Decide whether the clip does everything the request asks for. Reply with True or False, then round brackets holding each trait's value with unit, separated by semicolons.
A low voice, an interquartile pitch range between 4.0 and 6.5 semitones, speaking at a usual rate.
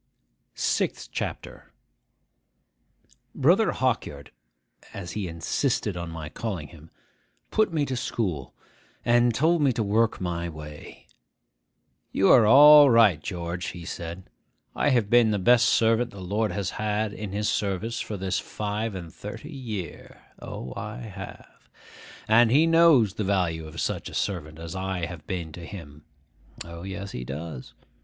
True (100 Hz; 5.3 semitones; 150 wpm)